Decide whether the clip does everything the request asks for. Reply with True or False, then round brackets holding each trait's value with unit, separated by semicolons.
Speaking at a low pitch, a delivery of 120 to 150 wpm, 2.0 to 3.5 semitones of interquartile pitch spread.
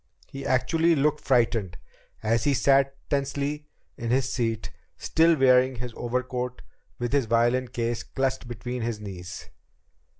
True (125 Hz; 140 wpm; 2.7 semitones)